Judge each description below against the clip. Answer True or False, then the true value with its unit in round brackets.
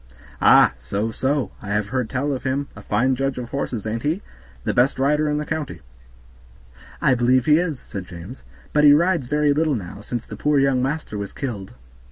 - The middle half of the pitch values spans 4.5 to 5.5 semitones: True (5.0 semitones)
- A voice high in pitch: False (130 Hz)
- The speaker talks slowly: False (200 wpm)